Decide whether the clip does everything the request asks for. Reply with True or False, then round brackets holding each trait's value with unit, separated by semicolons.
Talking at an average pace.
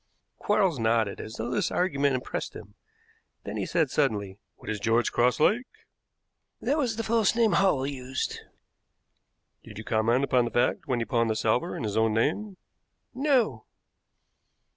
True (165 wpm)